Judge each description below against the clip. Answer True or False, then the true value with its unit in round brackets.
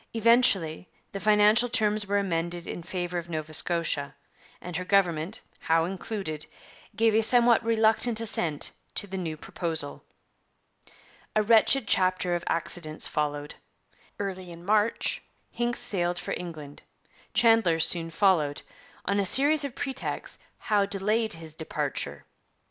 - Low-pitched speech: False (185 Hz)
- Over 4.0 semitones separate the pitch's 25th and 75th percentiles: True (4.8 semitones)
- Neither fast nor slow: False (130 wpm)